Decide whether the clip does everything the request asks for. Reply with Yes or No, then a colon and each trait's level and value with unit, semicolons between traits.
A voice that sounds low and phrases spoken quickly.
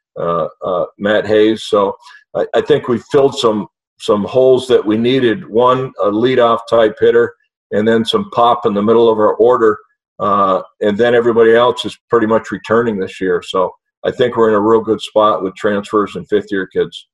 No: low, 120 Hz; average, 195 wpm